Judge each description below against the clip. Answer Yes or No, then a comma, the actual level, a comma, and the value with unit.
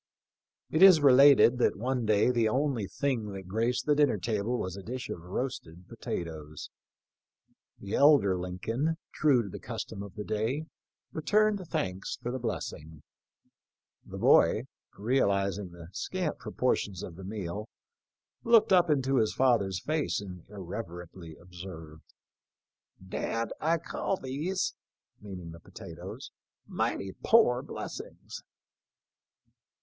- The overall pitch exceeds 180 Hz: No, low, 110 Hz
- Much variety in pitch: Yes, wide, 6.6 semitones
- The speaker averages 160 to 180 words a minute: No, average, 140 wpm